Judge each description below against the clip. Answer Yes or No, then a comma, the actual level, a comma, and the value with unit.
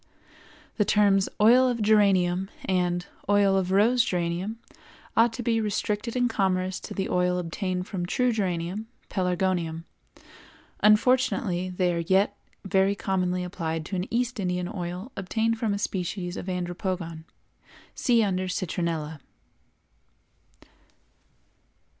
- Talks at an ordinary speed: No, slow, 125 wpm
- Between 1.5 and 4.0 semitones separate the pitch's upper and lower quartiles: Yes, average, 2.9 semitones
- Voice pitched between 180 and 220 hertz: Yes, high, 190 Hz